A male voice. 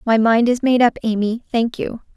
No: female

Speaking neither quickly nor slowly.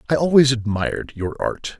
Yes: average, 165 wpm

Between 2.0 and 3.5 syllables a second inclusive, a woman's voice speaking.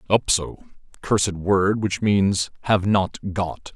No: 3.3 syllables/s; male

